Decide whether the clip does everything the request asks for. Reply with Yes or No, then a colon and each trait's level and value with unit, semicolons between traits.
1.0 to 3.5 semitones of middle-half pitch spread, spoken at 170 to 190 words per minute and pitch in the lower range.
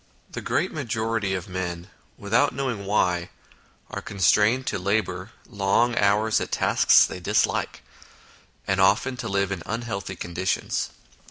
No: average, 3.1 semitones; slow, 135 wpm; low, 100 Hz